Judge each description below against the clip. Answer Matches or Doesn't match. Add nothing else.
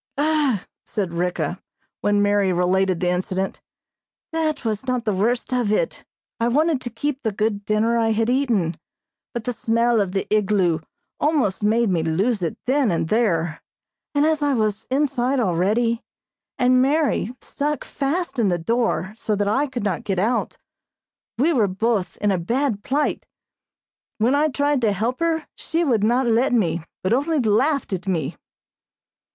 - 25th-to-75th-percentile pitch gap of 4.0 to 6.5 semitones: Matches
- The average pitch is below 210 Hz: Doesn't match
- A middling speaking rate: Matches